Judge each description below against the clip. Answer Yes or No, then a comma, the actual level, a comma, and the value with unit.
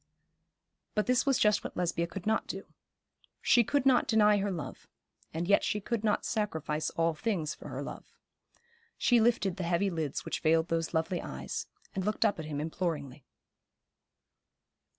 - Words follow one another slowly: No, average, 170 wpm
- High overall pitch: No, medium, 180 Hz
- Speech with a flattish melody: No, average, 4.7 semitones